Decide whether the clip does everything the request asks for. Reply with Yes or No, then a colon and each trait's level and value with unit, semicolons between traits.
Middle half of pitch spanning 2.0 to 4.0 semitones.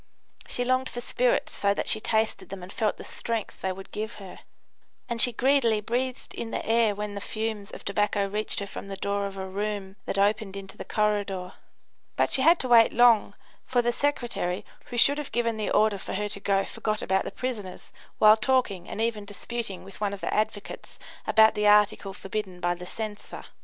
Yes: average, 2.7 semitones